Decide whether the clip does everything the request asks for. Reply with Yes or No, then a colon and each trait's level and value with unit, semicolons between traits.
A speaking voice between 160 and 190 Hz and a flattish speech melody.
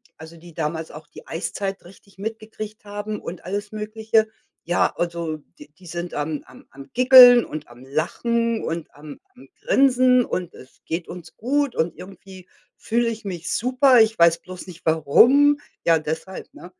No: medium, 185 Hz; wide, 5.5 semitones